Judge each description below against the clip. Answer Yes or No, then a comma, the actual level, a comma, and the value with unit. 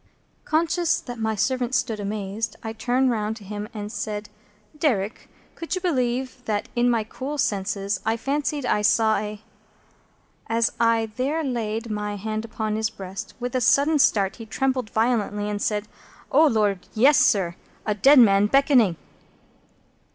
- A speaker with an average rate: Yes, average, 160 wpm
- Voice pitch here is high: Yes, high, 225 Hz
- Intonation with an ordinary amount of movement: Yes, average, 3.6 semitones